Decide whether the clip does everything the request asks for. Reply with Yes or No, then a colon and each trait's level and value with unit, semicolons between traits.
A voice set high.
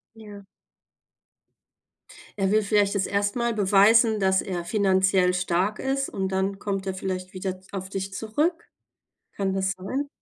Yes: high, 195 Hz